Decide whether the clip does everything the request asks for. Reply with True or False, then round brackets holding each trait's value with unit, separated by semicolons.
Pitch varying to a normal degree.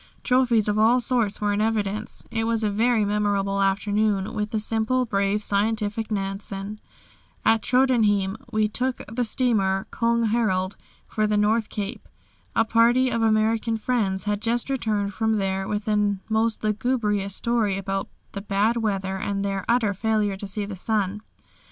False (2.2 semitones)